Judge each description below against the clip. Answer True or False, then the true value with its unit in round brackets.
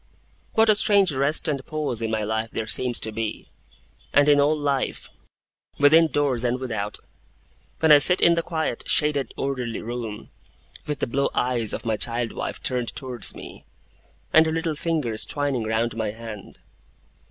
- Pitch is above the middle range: False (130 Hz)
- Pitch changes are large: False (4.8 semitones)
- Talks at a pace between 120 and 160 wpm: False (170 wpm)